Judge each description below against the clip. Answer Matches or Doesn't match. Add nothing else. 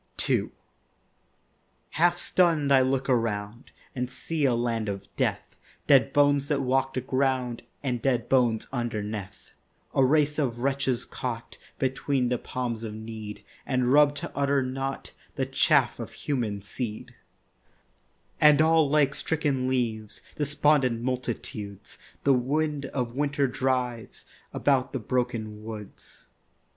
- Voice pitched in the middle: Doesn't match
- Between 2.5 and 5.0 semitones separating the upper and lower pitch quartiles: Matches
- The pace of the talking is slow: Matches